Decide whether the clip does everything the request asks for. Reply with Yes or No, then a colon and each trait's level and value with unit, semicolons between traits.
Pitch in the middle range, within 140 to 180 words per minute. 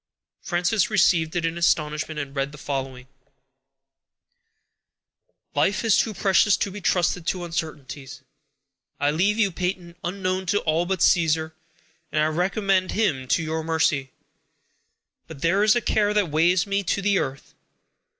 Yes: medium, 175 Hz; average, 150 wpm